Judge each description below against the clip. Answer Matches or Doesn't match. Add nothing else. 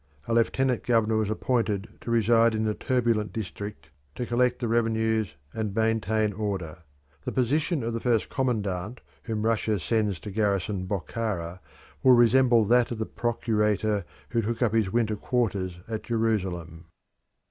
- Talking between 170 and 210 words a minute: Doesn't match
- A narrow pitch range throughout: Matches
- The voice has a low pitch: Matches